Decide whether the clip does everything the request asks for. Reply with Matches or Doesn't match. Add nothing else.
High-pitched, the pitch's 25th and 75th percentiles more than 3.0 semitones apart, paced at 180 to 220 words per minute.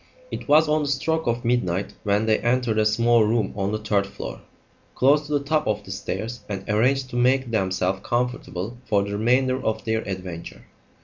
Doesn't match